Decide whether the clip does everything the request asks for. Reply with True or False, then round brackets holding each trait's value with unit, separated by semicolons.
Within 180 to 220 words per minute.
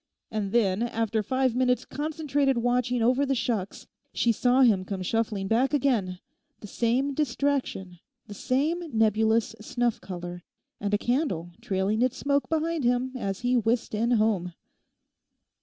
False (140 wpm)